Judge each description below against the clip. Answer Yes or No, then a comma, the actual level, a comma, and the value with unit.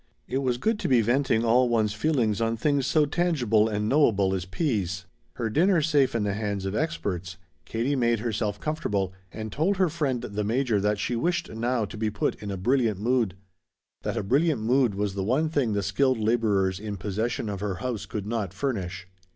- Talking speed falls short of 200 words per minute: No, fast, 205 wpm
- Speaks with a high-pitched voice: No, low, 115 Hz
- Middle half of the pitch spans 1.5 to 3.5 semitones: No, average, 4.6 semitones